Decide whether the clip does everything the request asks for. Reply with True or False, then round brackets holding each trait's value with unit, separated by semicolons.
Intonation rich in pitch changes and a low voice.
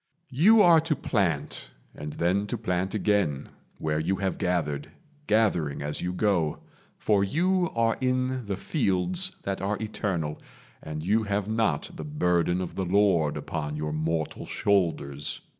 True (5.7 semitones; 95 Hz)